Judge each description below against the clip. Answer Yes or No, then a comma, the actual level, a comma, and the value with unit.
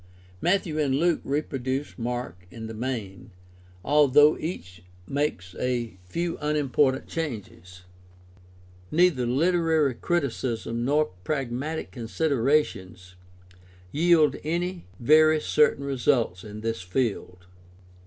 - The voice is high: No, low, 135 Hz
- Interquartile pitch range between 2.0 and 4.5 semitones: No, average, 5.3 semitones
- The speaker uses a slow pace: Yes, slow, 95 wpm